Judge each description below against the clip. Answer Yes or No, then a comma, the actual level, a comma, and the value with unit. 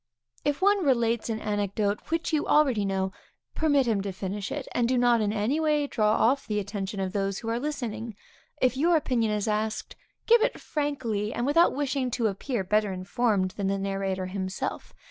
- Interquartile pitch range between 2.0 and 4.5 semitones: No, average, 5.3 semitones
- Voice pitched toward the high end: Yes, high, 225 Hz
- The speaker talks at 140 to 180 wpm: No, average, 190 wpm